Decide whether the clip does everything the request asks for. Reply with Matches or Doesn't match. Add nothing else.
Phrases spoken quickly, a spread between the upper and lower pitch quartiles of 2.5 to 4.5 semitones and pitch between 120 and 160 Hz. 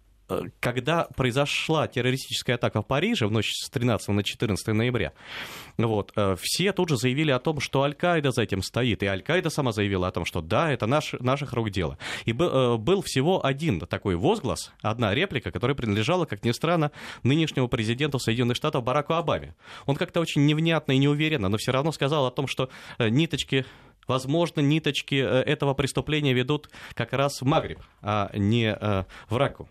Doesn't match